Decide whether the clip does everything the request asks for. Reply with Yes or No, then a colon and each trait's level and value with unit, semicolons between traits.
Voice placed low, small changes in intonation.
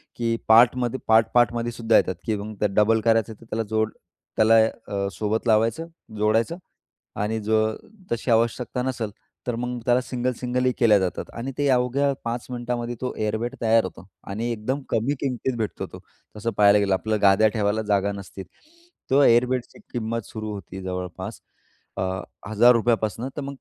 Yes: low, 115 Hz; narrow, 2.3 semitones